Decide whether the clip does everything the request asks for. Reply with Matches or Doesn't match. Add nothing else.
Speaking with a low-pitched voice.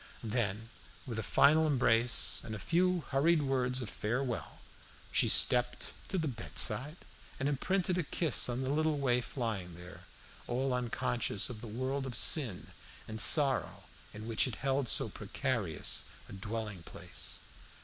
Matches